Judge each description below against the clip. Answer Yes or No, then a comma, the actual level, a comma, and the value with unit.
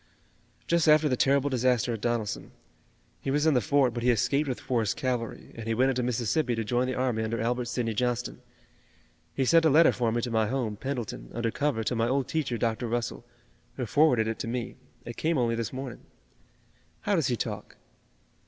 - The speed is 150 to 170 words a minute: No, fast, 205 wpm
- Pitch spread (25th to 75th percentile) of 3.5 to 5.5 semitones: No, average, 2.8 semitones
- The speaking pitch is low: Yes, low, 125 Hz